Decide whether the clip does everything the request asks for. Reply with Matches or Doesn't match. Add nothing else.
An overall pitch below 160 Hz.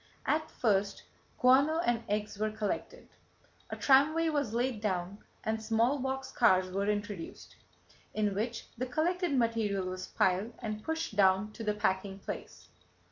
Doesn't match